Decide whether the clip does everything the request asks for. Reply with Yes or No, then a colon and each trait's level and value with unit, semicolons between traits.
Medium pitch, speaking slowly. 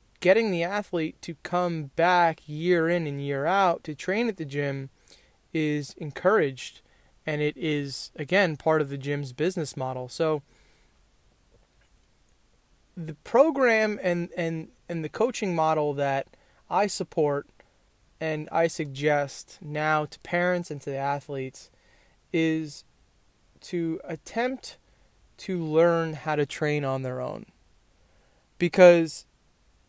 Yes: medium, 155 Hz; slow, 125 wpm